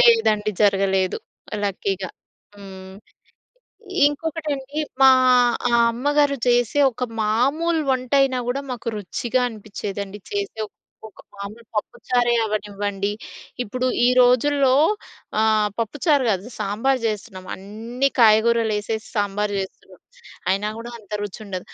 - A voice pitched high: Yes, high, 220 Hz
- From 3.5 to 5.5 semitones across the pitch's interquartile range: Yes, average, 4.2 semitones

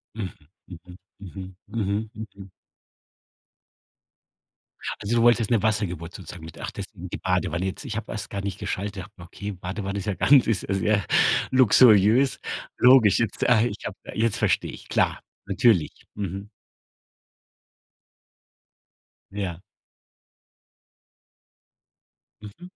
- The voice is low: Yes, low, 100 Hz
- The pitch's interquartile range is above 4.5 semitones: No, average, 2.8 semitones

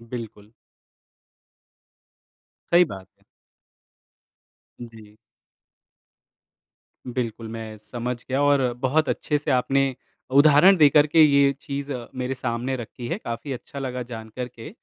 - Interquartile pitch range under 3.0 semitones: No, average, 3.4 semitones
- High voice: No, low, 125 Hz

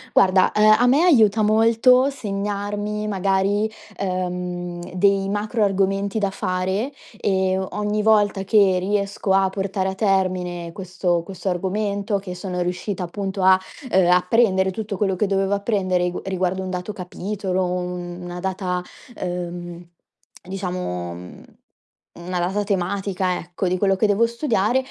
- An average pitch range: No, narrow, 2.2 semitones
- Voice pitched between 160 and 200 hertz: Yes, high, 190 Hz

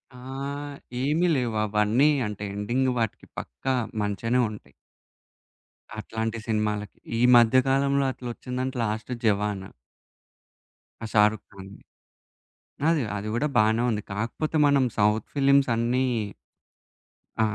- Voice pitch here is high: No, low, 115 Hz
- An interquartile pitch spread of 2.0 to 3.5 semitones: No, average, 4.0 semitones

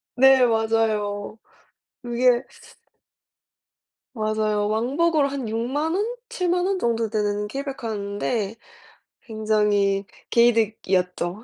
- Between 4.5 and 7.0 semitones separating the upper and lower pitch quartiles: No, average, 4.1 semitones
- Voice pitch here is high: Yes, high, 225 Hz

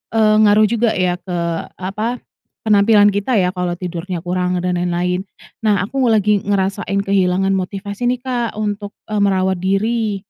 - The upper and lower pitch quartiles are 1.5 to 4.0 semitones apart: Yes, average, 2.7 semitones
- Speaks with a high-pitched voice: Yes, high, 200 Hz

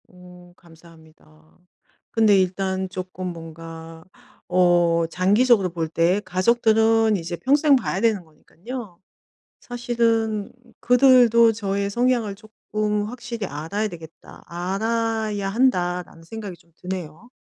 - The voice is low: No, high, 195 Hz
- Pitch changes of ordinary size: Yes, average, 4.6 semitones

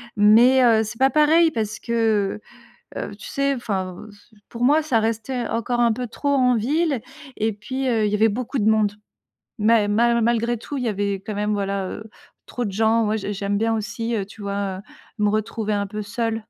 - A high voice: Yes, high, 220 Hz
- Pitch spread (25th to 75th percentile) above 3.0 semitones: No, narrow, 2.5 semitones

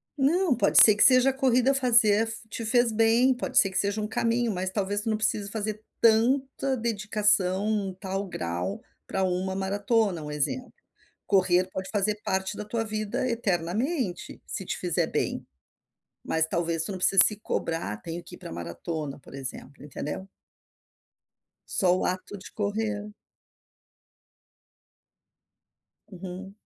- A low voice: No, high, 205 Hz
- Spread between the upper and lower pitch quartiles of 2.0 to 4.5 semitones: Yes, average, 3.7 semitones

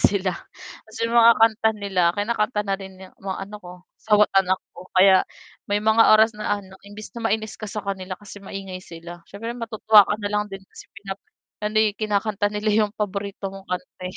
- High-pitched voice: Yes, high, 205 Hz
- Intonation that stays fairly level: Yes, narrow, 1.9 semitones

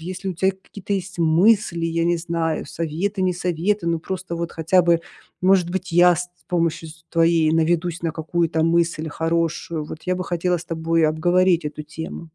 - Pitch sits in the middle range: Yes, medium, 170 Hz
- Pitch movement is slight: Yes, narrow, 1.8 semitones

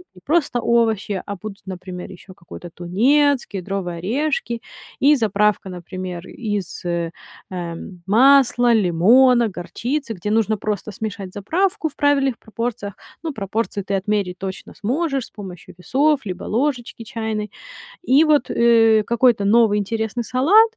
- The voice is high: Yes, high, 220 Hz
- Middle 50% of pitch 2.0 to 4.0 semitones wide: No, average, 4.9 semitones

